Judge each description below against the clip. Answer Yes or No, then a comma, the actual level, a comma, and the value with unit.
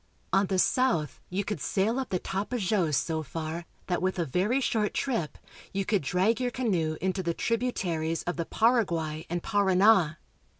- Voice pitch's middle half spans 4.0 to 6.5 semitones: Yes, average, 4.8 semitones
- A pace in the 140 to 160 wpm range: No, average, 170 wpm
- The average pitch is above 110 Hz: Yes, medium, 185 Hz